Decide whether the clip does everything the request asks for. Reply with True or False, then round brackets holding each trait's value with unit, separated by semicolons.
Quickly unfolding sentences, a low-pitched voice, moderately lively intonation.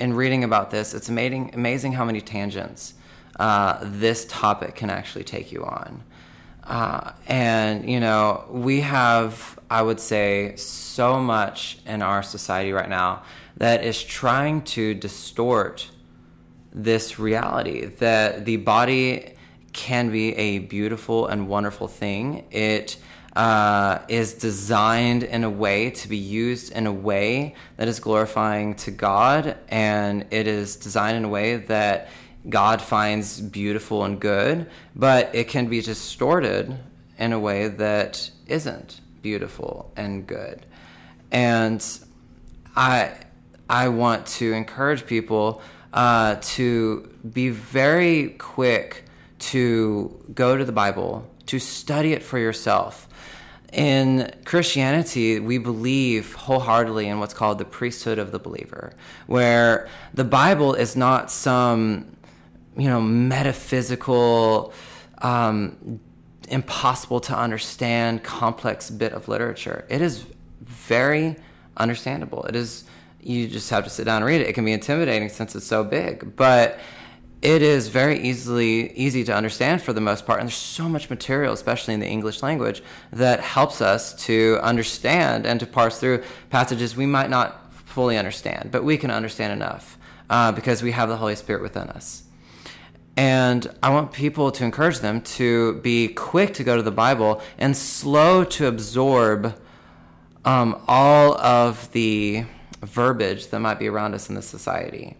False (145 wpm; 115 Hz; 3.1 semitones)